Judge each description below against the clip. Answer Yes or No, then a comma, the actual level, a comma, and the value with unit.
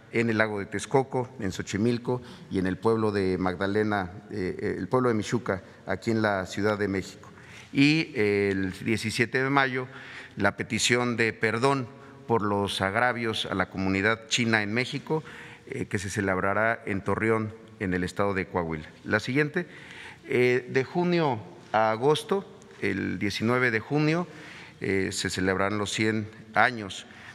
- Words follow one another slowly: No, average, 145 wpm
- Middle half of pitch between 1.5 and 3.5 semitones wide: No, average, 4.3 semitones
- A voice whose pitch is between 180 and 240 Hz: No, low, 110 Hz